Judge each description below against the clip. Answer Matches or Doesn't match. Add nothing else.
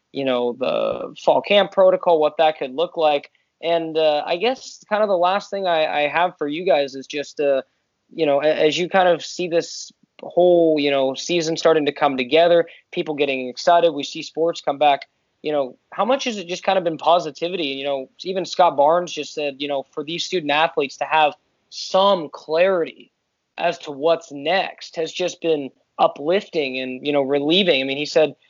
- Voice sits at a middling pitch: Matches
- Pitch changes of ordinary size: Matches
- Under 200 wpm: Doesn't match